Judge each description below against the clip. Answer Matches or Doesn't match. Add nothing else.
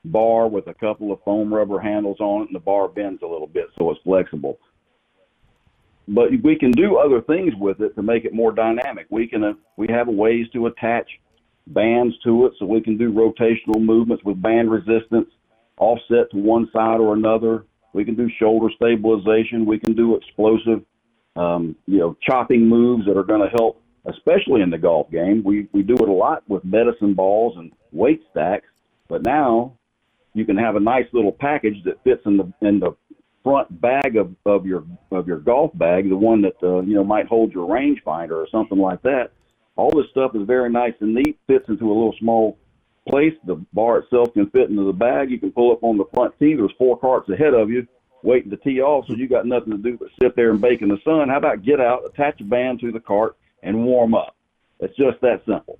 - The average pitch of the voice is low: Matches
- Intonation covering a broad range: Doesn't match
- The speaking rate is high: Matches